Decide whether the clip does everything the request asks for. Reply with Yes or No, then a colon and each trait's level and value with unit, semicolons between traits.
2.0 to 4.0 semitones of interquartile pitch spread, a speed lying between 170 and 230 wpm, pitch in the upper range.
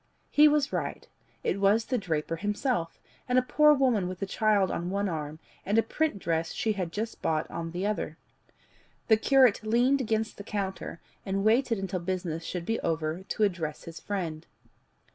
No: average, 5.0 semitones; average, 180 wpm; high, 200 Hz